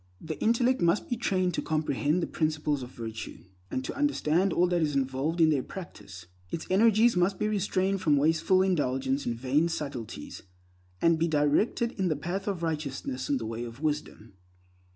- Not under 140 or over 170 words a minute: No, average, 180 wpm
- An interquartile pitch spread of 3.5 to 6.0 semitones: Yes, wide, 5.5 semitones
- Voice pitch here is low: No, medium, 155 Hz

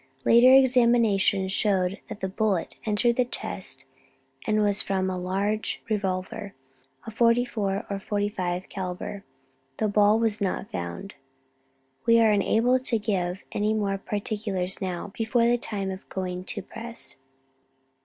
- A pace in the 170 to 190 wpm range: No, slow, 135 wpm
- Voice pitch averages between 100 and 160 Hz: No, high, 205 Hz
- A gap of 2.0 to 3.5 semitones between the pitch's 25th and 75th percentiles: Yes, average, 2.8 semitones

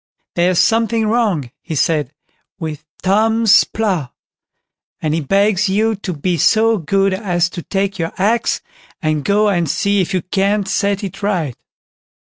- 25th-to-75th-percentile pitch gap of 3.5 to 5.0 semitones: Yes, average, 3.8 semitones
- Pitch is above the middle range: Yes, high, 195 Hz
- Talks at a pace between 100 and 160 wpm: Yes, average, 150 wpm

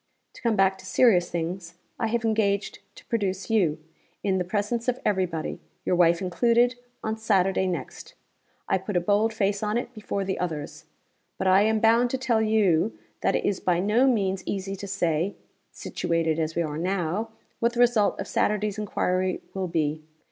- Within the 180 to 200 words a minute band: Yes, average, 185 wpm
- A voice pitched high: Yes, high, 195 Hz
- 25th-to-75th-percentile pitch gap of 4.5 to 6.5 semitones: No, average, 3.8 semitones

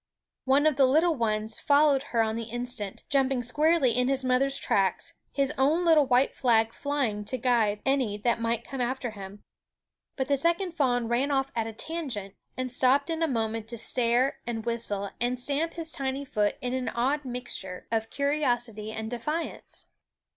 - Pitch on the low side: No, very high, 250 Hz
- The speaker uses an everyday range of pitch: Yes, average, 3.6 semitones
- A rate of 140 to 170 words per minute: No, average, 180 wpm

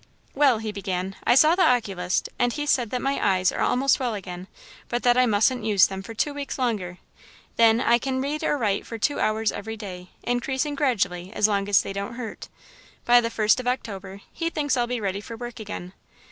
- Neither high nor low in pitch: No, high, 230 Hz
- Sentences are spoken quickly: Yes, fast, 215 wpm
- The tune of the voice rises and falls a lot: No, average, 4.2 semitones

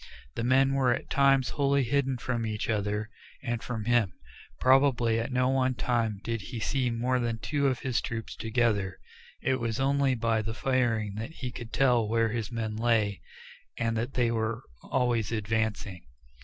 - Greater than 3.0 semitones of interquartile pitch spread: No, narrow, 2.6 semitones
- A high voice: No, low, 120 Hz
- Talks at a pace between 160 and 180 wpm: Yes, average, 175 wpm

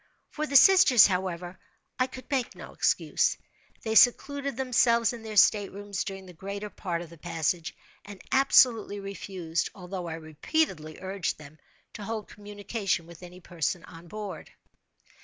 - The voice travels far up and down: No, average, 4.6 semitones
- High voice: Yes, high, 195 Hz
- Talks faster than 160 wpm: No, average, 150 wpm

